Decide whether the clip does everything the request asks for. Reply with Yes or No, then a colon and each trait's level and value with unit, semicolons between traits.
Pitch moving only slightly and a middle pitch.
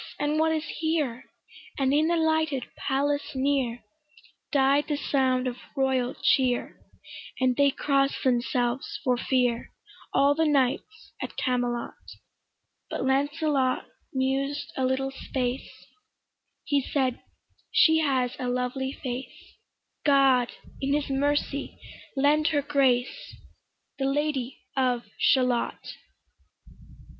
No: narrow, 2.2 semitones; very high, 270 Hz